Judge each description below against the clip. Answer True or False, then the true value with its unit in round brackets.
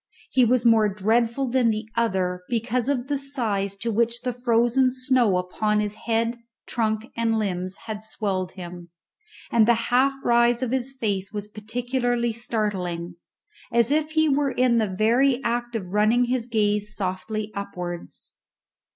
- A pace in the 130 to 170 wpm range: True (155 wpm)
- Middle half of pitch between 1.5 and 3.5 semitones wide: True (2.9 semitones)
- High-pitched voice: True (230 Hz)